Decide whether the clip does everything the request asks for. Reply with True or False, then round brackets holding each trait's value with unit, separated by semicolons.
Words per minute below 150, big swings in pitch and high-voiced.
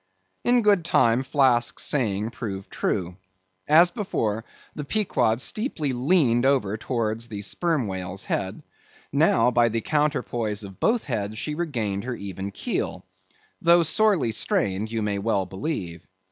False (140 wpm; 6.8 semitones; 115 Hz)